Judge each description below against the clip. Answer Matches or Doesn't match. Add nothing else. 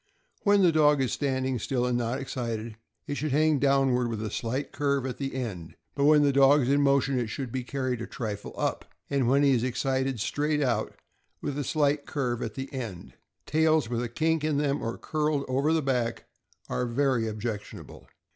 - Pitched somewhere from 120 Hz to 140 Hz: Matches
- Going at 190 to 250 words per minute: Matches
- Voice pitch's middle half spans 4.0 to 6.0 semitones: Doesn't match